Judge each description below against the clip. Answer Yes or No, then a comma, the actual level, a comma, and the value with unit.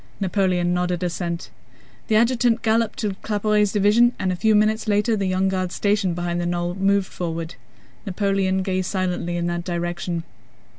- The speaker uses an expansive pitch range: No, average, 3.1 semitones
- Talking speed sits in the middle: Yes, average, 160 wpm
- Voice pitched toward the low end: No, high, 190 Hz